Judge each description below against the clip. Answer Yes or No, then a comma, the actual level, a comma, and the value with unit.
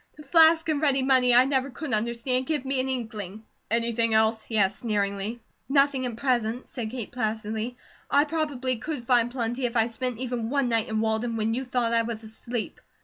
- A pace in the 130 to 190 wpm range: No, average, 200 wpm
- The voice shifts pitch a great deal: No, average, 2.9 semitones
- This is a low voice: No, high, 240 Hz